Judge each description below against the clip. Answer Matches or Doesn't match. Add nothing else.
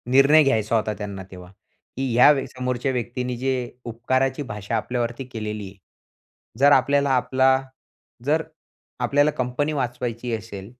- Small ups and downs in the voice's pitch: Doesn't match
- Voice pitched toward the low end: Matches